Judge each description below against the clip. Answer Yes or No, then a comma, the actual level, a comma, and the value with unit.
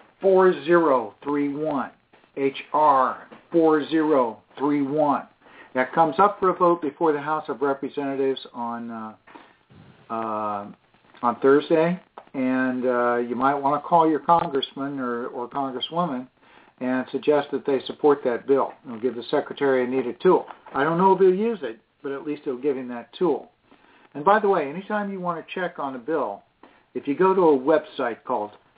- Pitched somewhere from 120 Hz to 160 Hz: Yes, medium, 140 Hz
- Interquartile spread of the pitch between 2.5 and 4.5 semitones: Yes, average, 4.2 semitones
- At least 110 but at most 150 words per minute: No, average, 165 wpm